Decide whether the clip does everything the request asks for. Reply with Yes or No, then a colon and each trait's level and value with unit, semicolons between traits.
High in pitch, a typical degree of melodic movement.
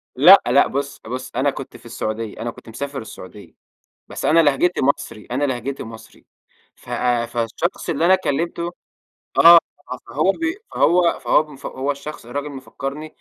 No: medium, 140 Hz; average, 4.5 semitones